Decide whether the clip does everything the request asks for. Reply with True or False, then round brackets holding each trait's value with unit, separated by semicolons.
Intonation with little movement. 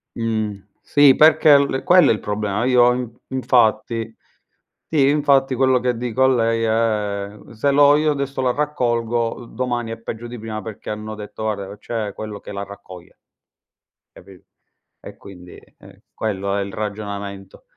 False (3.8 semitones)